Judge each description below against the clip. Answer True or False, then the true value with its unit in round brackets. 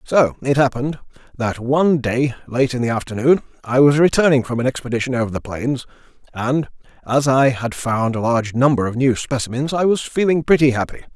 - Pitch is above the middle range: False (130 Hz)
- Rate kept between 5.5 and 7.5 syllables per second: True (5.7 syllables/s)